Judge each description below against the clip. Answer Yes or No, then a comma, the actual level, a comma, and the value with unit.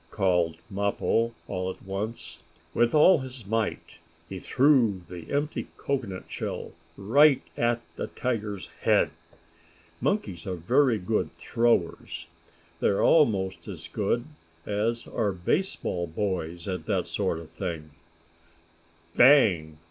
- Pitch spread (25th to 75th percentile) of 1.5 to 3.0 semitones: No, average, 4.7 semitones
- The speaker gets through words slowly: Yes, slow, 120 wpm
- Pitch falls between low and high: No, low, 100 Hz